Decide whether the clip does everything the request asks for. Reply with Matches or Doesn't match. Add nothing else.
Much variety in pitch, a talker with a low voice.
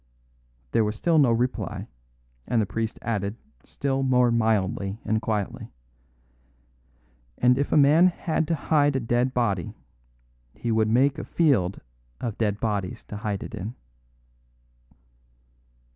Doesn't match